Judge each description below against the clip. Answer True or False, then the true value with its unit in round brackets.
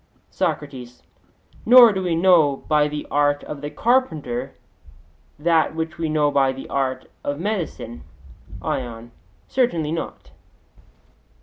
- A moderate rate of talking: False (120 wpm)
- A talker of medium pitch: True (150 Hz)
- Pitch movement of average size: True (3.7 semitones)